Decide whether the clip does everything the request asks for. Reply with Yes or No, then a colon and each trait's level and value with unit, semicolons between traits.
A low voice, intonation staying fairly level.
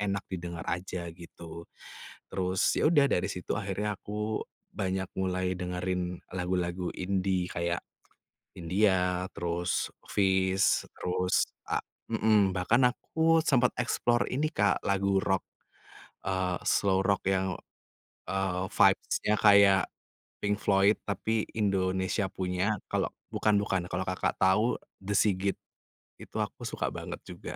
Yes: very low, 95 Hz; narrow, 2.0 semitones